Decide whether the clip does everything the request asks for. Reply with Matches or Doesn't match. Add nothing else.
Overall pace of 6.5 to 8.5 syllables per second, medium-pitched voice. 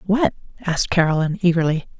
Matches